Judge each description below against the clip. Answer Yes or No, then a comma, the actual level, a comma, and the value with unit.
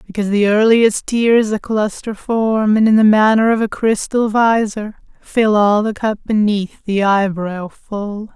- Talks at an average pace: Yes, average, 165 wpm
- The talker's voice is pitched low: No, high, 215 Hz